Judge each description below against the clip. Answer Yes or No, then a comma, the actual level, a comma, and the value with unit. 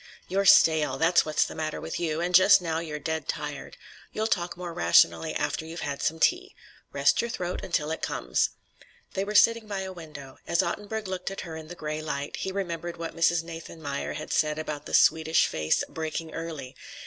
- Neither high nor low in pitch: Yes, medium, 165 Hz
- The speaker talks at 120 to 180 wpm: No, average, 200 wpm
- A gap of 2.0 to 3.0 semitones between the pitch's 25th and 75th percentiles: Yes, narrow, 2.6 semitones